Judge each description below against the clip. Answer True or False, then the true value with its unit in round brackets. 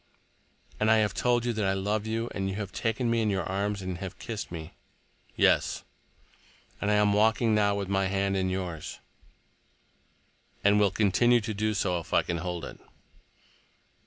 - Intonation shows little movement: True (2.2 semitones)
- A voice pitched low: True (100 Hz)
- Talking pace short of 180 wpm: False (185 wpm)